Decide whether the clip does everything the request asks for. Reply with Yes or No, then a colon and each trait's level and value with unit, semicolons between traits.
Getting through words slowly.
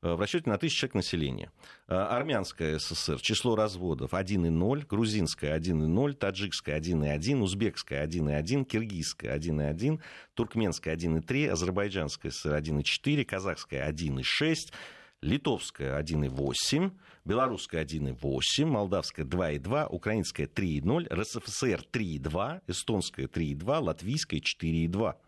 Yes: slow, 95 wpm